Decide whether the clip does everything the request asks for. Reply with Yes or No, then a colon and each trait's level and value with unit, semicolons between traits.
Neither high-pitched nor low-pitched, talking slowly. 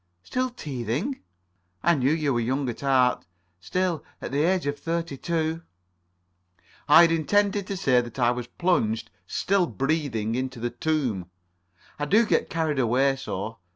No: medium, 145 Hz; average, 155 wpm